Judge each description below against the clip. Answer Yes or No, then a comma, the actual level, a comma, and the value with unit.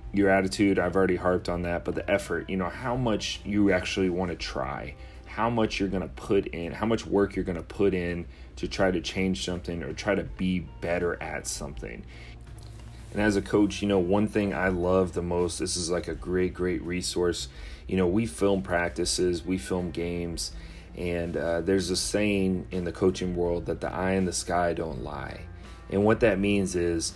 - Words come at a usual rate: No, fast, 210 wpm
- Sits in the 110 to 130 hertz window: No, very low, 90 Hz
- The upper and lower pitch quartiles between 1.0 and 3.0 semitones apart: Yes, narrow, 2.4 semitones